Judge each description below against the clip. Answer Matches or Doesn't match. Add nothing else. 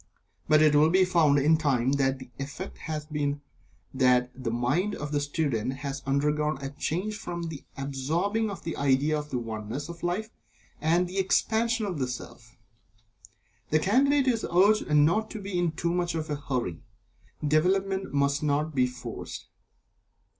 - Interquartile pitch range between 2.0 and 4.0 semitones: Doesn't match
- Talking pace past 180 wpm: Doesn't match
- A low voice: Doesn't match